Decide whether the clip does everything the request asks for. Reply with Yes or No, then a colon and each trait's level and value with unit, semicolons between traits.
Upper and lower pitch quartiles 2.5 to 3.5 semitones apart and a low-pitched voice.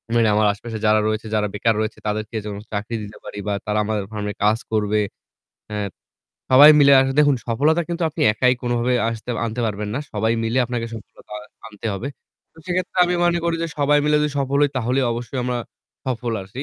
No: average, 4.5 semitones; low, 115 Hz